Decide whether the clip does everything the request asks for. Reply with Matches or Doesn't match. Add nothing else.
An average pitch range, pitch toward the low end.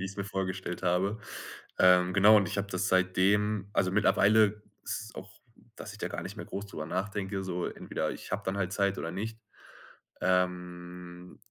Doesn't match